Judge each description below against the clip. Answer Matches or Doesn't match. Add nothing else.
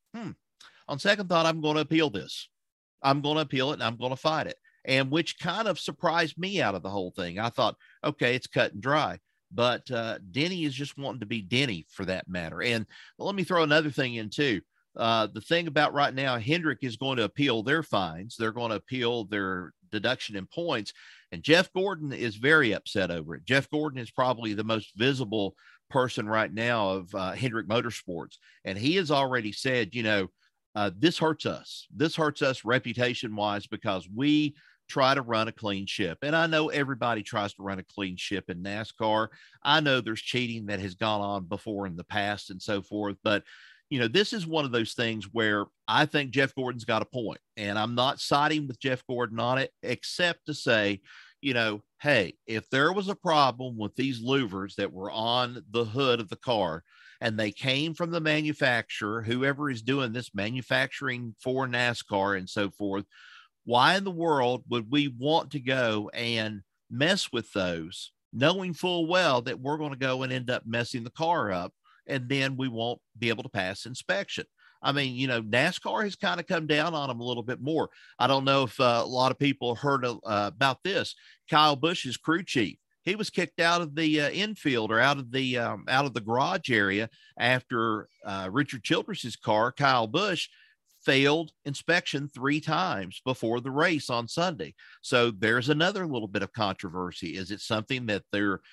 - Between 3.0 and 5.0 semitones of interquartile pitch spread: Doesn't match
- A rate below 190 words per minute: Doesn't match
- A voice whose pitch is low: Matches